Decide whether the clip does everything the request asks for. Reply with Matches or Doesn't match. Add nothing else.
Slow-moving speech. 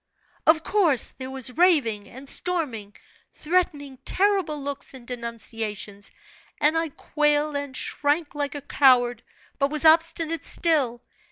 Matches